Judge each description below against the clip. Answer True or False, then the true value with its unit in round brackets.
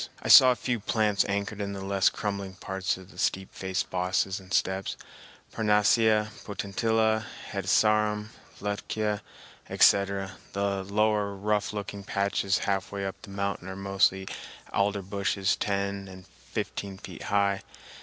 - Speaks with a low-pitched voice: True (100 Hz)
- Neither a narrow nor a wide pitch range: False (1.5 semitones)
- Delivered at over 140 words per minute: False (135 wpm)